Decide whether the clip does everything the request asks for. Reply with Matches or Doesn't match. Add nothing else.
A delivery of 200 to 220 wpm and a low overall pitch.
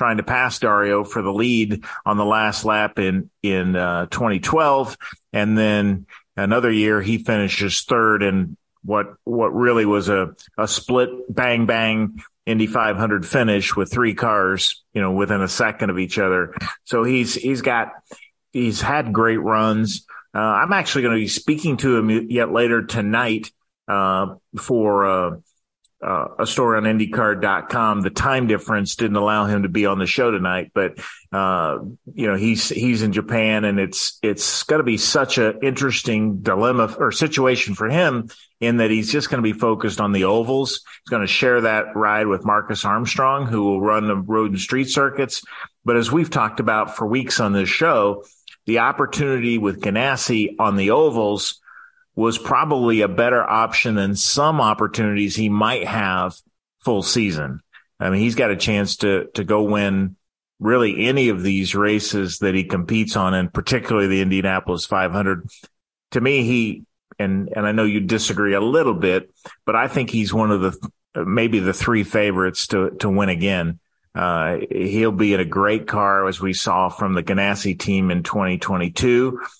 Doesn't match